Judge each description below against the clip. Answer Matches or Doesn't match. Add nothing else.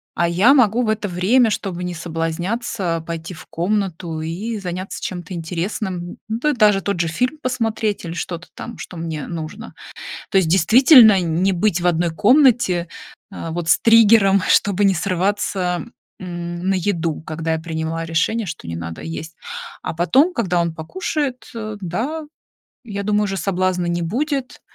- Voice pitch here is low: Doesn't match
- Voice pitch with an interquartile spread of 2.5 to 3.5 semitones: Doesn't match